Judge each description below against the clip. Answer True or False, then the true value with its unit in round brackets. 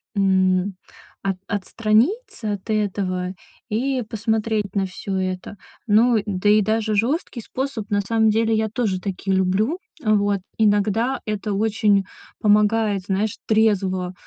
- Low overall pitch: False (210 Hz)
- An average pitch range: False (2.2 semitones)